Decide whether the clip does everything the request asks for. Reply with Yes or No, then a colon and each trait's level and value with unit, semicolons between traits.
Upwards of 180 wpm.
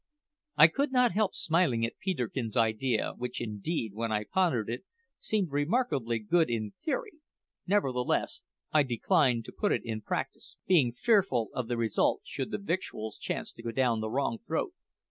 No: average, 165 wpm